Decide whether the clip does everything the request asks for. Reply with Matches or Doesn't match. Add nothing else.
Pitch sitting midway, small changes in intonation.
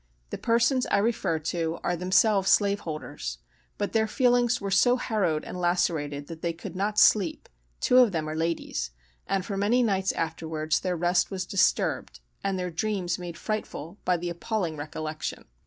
Doesn't match